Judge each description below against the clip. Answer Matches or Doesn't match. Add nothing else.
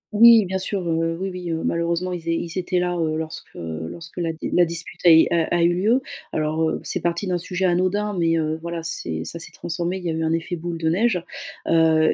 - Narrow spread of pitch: Matches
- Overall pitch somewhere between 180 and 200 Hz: Doesn't match